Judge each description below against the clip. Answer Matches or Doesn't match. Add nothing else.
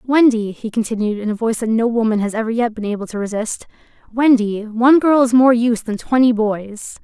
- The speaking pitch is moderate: Doesn't match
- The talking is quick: Matches